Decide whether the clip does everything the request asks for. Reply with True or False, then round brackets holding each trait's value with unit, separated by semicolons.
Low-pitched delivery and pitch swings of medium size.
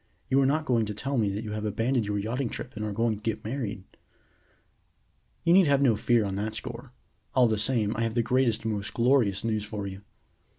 True (115 Hz; 3.2 semitones)